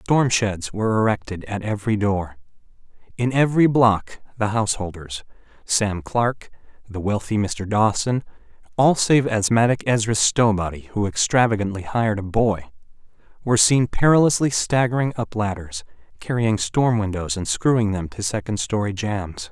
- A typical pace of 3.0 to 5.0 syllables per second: Yes, 4.9 syllables/s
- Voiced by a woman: No, male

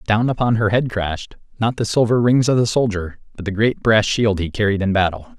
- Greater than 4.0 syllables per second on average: Yes, 5.5 syllables/s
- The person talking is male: Yes, male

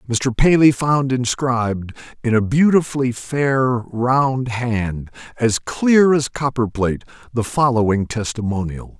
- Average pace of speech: No, slow, 115 wpm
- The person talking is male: Yes, male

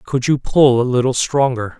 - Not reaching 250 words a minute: Yes, average, 200 wpm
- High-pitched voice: No, low, 130 Hz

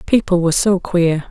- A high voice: No, medium, 180 Hz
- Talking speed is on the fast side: No, average, 185 wpm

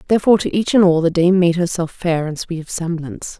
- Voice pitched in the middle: Yes, medium, 175 Hz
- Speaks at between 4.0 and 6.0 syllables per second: No, 6.3 syllables/s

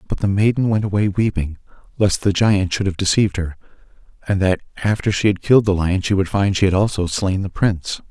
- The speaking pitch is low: Yes, very low, 95 Hz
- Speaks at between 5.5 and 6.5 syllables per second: Yes, 6.0 syllables/s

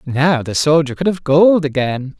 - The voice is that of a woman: No, male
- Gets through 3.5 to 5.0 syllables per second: Yes, 4.4 syllables/s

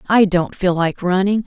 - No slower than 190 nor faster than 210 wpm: Yes, fast, 205 wpm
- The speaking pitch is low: No, high, 190 Hz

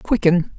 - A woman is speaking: Yes, female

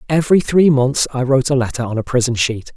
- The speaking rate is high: Yes, fast, 240 wpm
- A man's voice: Yes, male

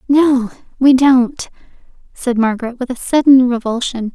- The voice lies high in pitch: Yes, very high, 250 Hz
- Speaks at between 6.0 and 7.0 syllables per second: No, 4.6 syllables/s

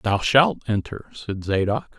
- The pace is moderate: Yes, average, 150 wpm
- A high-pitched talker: No, low, 110 Hz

